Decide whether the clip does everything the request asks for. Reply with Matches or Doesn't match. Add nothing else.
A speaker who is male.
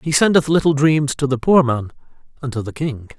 Matches